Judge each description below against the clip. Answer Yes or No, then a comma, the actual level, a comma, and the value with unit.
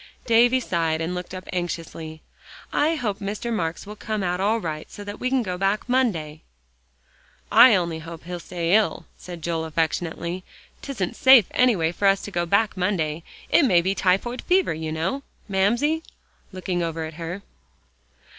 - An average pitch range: Yes, average, 4.6 semitones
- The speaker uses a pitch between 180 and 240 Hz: Yes, medium, 185 Hz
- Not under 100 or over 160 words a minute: No, average, 170 wpm